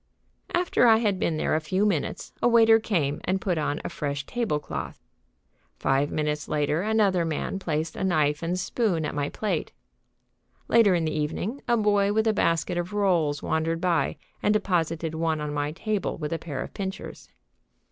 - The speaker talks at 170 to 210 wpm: Yes, average, 185 wpm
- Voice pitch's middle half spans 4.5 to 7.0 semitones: Yes, wide, 5.4 semitones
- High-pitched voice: No, medium, 170 Hz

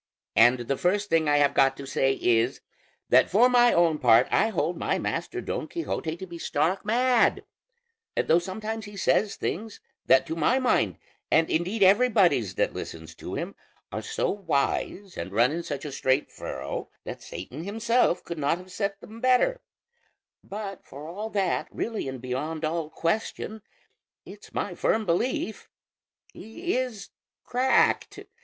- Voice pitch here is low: No, medium, 185 Hz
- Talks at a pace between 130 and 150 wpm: No, average, 160 wpm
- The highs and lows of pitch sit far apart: Yes, wide, 6.7 semitones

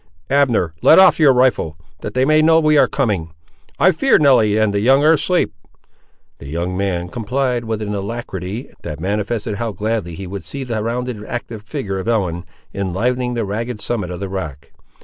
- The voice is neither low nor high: No, low, 110 Hz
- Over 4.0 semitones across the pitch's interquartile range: Yes, average, 4.7 semitones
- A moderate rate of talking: Yes, average, 190 wpm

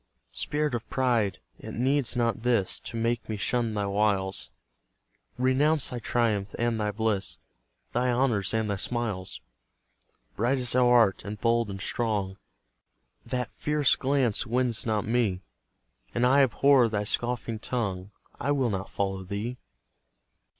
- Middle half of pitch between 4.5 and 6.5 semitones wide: No, average, 3.3 semitones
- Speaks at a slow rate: No, average, 145 wpm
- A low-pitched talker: Yes, low, 115 Hz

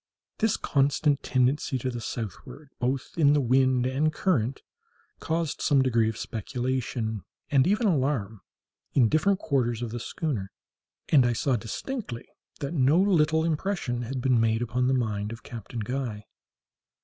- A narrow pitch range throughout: No, average, 4.1 semitones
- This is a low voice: Yes, low, 130 Hz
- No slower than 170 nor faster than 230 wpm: No, average, 155 wpm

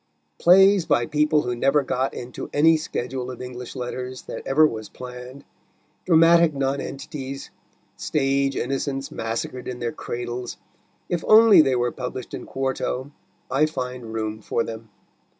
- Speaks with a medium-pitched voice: No, low, 130 Hz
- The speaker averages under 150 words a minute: Yes, average, 140 wpm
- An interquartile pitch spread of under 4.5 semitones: Yes, average, 3.1 semitones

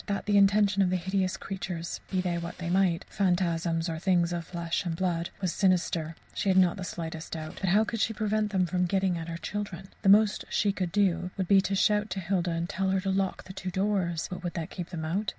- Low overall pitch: No, medium, 185 Hz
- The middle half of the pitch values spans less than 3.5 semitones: Yes, narrow, 2.4 semitones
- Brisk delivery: Yes, fast, 240 wpm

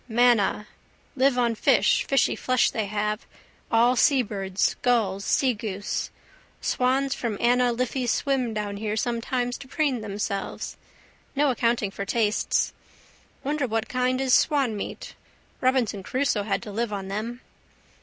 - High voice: Yes, high, 235 Hz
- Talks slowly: Yes, slow, 130 wpm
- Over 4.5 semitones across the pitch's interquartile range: No, average, 3.3 semitones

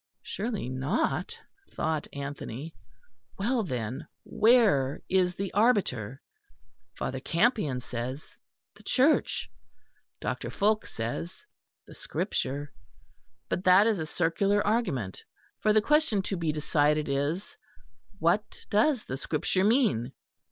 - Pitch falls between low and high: Yes, medium, 170 Hz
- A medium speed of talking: No, slow, 110 wpm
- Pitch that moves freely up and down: Yes, wide, 7.6 semitones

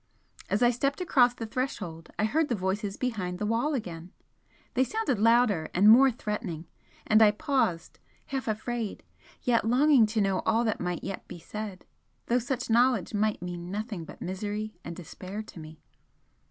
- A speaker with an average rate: Yes, average, 170 wpm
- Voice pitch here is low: No, high, 215 Hz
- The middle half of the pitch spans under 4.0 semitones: No, average, 4.7 semitones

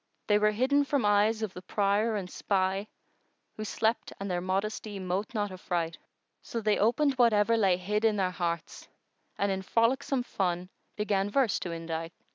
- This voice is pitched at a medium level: No, high, 205 Hz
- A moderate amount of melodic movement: Yes, average, 3.0 semitones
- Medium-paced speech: Yes, average, 180 wpm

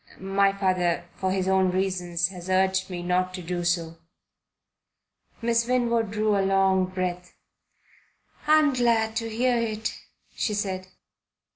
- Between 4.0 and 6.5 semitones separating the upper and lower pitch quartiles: No, average, 3.2 semitones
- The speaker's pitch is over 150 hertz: Yes, high, 190 Hz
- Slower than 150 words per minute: Yes, slow, 135 wpm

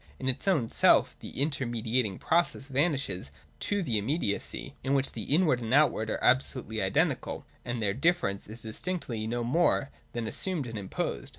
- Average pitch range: Yes, average, 4.9 semitones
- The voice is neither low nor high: No, low, 125 Hz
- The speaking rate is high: No, average, 170 wpm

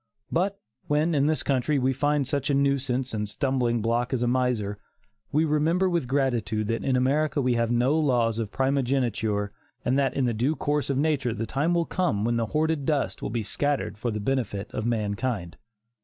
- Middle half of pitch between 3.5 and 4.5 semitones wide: Yes, average, 4.0 semitones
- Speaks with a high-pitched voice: No, low, 130 Hz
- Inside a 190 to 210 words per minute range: Yes, average, 200 wpm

